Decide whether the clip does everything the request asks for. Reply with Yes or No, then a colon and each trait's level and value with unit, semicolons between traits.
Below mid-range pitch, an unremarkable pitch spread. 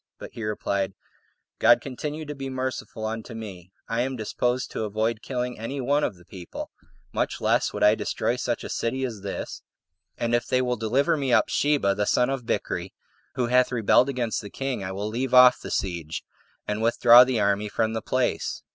Yes: low, 120 Hz; average, 3.3 semitones